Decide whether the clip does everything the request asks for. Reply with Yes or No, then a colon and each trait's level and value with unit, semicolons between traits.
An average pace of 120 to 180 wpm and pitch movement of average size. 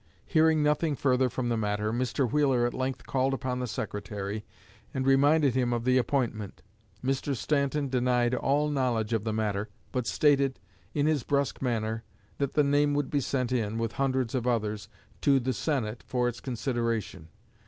Yes: average, 175 wpm; average, 3.4 semitones